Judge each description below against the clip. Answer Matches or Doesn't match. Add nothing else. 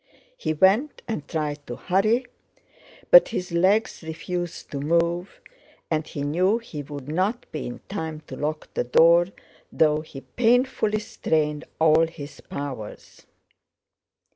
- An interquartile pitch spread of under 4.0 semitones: Doesn't match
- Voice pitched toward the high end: Doesn't match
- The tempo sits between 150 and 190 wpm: Doesn't match